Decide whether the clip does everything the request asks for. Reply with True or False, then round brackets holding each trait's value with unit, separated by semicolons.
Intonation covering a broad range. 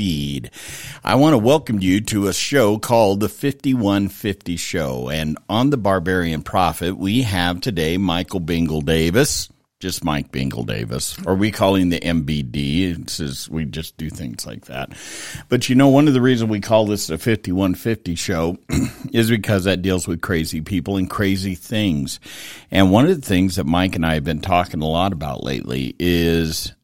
False (3.9 semitones)